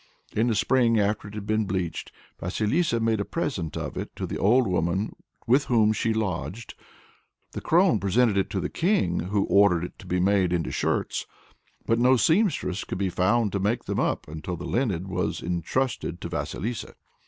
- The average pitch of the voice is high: No, low, 105 Hz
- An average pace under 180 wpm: No, average, 190 wpm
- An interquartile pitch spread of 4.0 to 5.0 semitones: Yes, average, 4.4 semitones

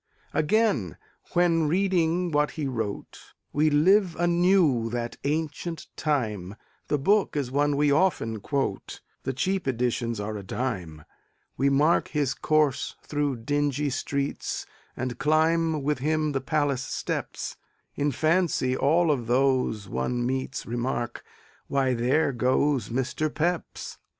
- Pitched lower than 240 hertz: Yes, medium, 140 Hz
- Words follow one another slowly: Yes, slow, 130 wpm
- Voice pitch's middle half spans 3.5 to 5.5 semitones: Yes, average, 4.1 semitones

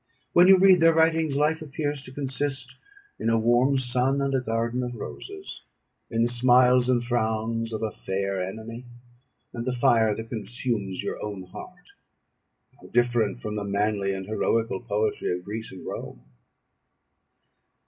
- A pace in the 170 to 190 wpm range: No, average, 160 wpm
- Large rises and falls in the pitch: No, average, 3.5 semitones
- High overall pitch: No, low, 120 Hz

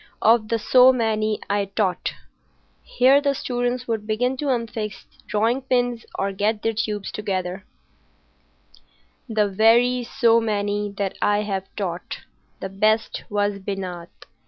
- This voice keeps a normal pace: No, slow, 125 wpm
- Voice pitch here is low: No, high, 215 Hz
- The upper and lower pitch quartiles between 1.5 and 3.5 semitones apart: Yes, average, 2.9 semitones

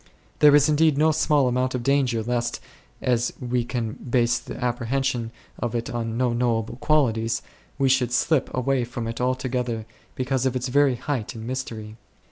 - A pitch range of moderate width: No, narrow, 2.1 semitones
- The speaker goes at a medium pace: Yes, average, 170 wpm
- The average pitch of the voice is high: No, low, 125 Hz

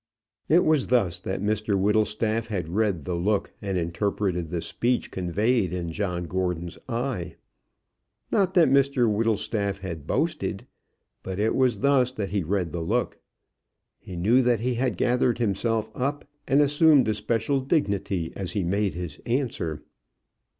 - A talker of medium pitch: No, low, 105 Hz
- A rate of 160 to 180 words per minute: No, average, 150 wpm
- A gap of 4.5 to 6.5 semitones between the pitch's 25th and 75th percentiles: Yes, average, 5.2 semitones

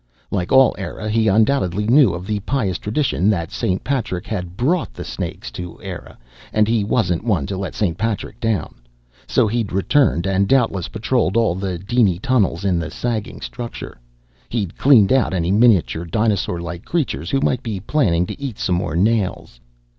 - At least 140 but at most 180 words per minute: Yes, average, 175 wpm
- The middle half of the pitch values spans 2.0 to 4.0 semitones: No, average, 4.5 semitones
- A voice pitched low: Yes, low, 105 Hz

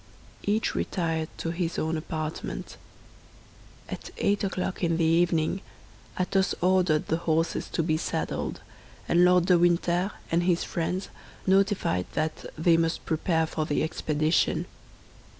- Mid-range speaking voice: Yes, medium, 170 Hz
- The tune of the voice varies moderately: No, narrow, 2.2 semitones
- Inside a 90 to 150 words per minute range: Yes, slow, 135 wpm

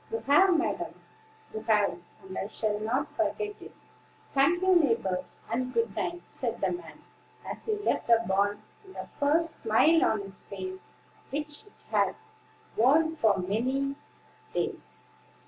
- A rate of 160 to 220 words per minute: No, average, 150 wpm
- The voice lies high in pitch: Yes, very high, 275 Hz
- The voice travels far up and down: Yes, wide, 8.1 semitones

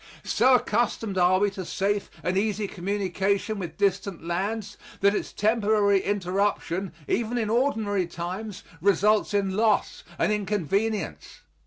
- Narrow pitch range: Yes, narrow, 2.0 semitones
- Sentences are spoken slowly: Yes, slow, 130 wpm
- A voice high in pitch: Yes, high, 200 Hz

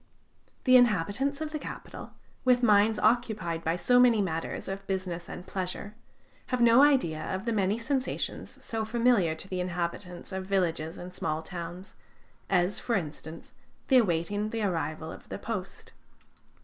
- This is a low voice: No, high, 195 Hz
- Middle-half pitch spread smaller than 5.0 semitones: No, average, 5.3 semitones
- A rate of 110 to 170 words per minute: Yes, average, 155 wpm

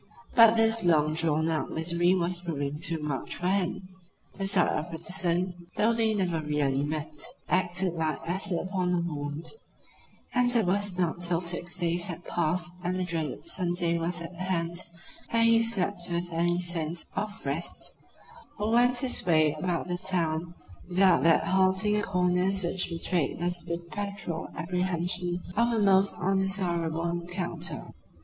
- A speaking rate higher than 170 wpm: No, average, 155 wpm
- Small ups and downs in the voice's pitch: Yes, narrow, 2.2 semitones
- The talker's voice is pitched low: No, medium, 175 Hz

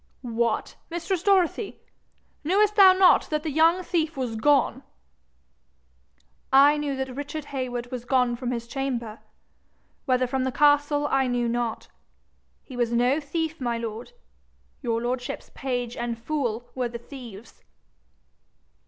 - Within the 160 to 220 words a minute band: No, slow, 135 wpm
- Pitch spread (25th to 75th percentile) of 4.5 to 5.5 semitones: No, average, 3.7 semitones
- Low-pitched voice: No, very high, 260 Hz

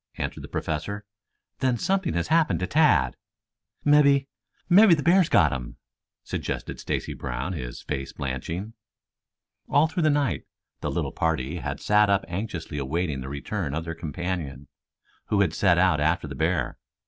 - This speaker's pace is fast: No, average, 160 wpm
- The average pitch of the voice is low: Yes, very low, 90 Hz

